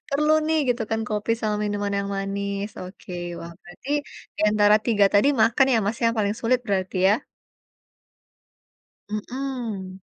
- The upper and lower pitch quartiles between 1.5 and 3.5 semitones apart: Yes, average, 2.8 semitones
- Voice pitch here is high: Yes, high, 210 Hz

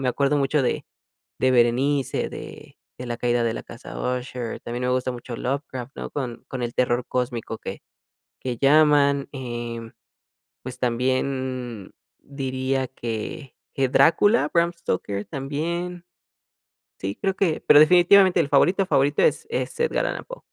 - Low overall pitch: Yes, low, 130 Hz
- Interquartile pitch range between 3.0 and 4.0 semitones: Yes, average, 3.5 semitones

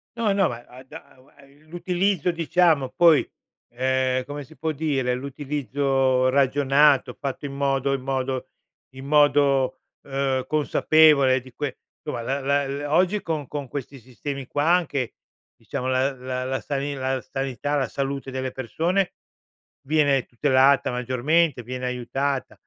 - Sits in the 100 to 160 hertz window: Yes, low, 135 Hz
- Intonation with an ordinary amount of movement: No, narrow, 2.1 semitones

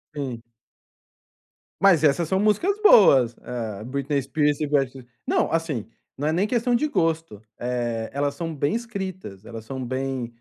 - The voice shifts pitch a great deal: Yes, wide, 6.1 semitones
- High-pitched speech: No, medium, 145 Hz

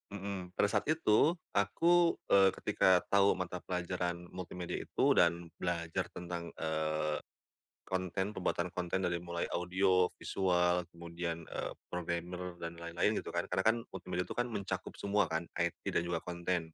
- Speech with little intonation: Yes, narrow, 1.9 semitones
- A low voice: Yes, very low, 90 Hz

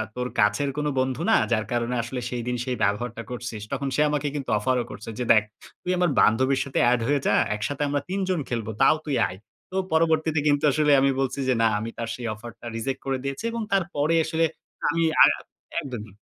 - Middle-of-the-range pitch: No, low, 130 Hz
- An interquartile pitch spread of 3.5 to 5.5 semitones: Yes, average, 4.0 semitones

